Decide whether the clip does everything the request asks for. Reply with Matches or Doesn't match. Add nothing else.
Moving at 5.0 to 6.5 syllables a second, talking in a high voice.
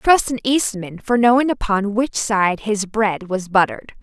Doesn't match